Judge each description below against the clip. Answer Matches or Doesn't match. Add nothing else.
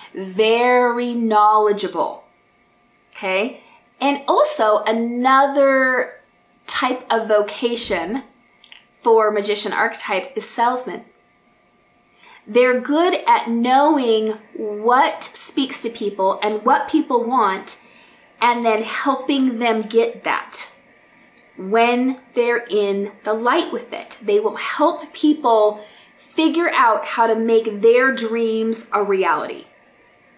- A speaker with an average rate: Doesn't match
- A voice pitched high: Matches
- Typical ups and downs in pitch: Matches